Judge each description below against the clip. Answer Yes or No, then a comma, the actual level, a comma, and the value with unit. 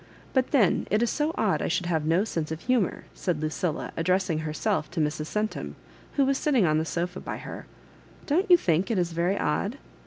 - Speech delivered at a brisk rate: Yes, fast, 220 wpm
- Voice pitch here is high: No, medium, 180 Hz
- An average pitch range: No, wide, 5.9 semitones